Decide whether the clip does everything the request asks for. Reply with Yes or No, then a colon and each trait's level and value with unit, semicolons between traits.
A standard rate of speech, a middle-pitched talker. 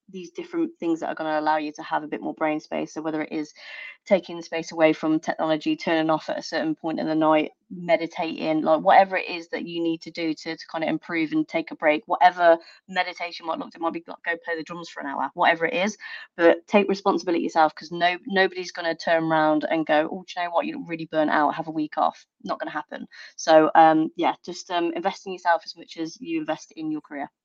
No: fast, 260 wpm; medium, 165 Hz